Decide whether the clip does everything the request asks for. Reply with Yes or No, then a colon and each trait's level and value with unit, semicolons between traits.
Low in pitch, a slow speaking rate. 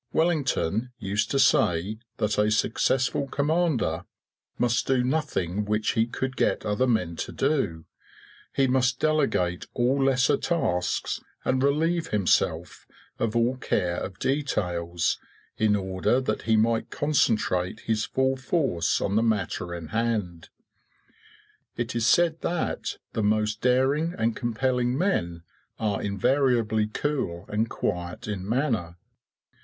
Yes: low, 115 Hz; slow, 130 wpm